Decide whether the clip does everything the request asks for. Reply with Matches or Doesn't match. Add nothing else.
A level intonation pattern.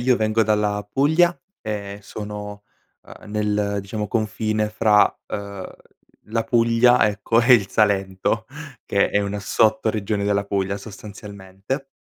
Matches